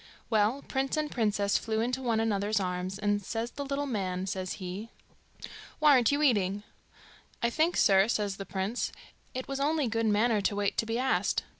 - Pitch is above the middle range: Yes, high, 220 Hz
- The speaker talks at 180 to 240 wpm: Yes, average, 185 wpm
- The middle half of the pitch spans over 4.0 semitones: Yes, average, 4.4 semitones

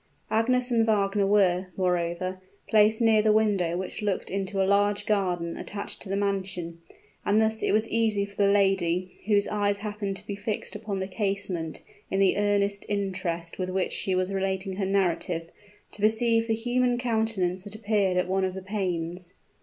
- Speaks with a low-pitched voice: No, high, 200 Hz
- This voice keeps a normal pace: Yes, average, 180 wpm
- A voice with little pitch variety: Yes, narrow, 2.3 semitones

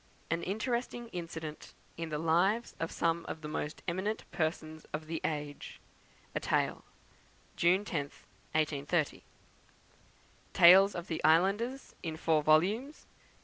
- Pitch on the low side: No, medium, 165 Hz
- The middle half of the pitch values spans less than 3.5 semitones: No, average, 3.8 semitones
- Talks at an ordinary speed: No, slow, 125 wpm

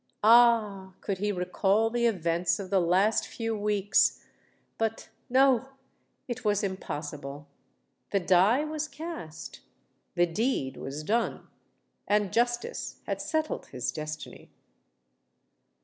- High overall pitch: Yes, high, 205 Hz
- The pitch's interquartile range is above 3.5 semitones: Yes, average, 5.3 semitones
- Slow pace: Yes, slow, 95 wpm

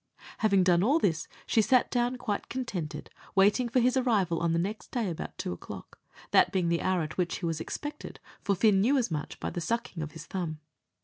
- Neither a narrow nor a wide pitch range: No, wide, 5.9 semitones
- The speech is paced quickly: Yes, fast, 215 wpm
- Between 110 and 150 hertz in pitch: No, high, 190 Hz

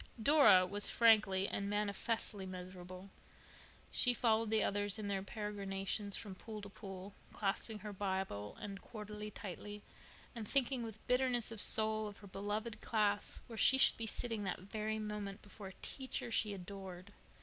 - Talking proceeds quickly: No, average, 160 wpm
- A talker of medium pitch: No, high, 205 Hz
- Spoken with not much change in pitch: Yes, narrow, 2.1 semitones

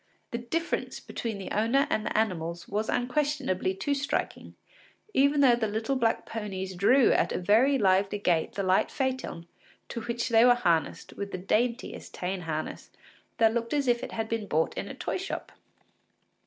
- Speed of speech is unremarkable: Yes, average, 180 wpm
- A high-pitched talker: Yes, high, 225 Hz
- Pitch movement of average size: Yes, average, 4.7 semitones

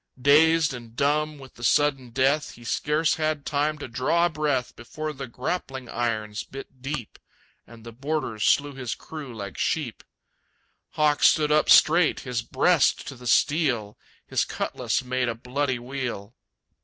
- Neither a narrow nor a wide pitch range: Yes, average, 4.0 semitones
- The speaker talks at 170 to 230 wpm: No, average, 155 wpm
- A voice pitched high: No, low, 135 Hz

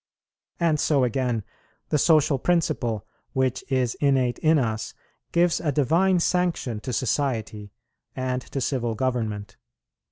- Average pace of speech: No, slow, 125 wpm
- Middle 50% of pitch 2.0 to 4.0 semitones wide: No, average, 4.5 semitones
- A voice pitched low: Yes, low, 130 Hz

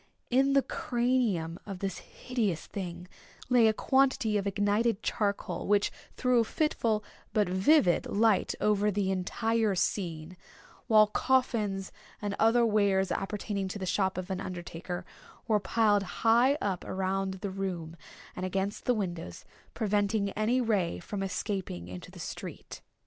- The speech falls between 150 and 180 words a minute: No, average, 140 wpm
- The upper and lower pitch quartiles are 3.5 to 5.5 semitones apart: No, average, 3.1 semitones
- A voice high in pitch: Yes, high, 200 Hz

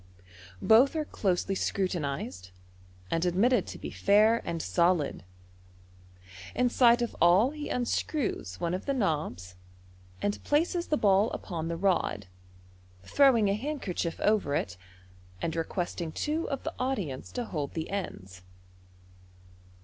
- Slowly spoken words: Yes, slow, 130 wpm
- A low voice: No, high, 195 Hz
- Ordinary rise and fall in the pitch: No, wide, 7.0 semitones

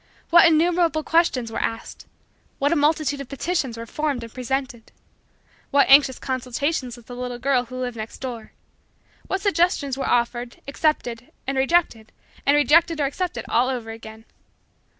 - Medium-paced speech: Yes, average, 155 wpm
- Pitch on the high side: Yes, very high, 265 Hz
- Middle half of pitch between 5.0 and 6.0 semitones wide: No, average, 4.3 semitones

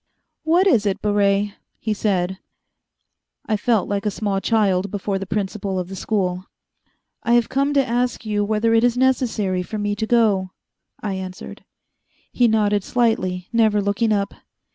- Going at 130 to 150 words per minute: No, average, 165 wpm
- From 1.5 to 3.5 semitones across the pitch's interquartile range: Yes, average, 2.8 semitones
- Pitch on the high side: Yes, high, 205 Hz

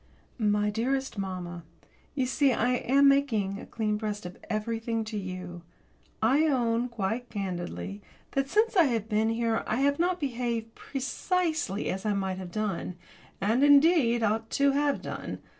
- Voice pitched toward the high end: Yes, high, 225 Hz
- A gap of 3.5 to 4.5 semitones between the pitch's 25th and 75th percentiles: No, average, 4.9 semitones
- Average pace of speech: Yes, average, 160 wpm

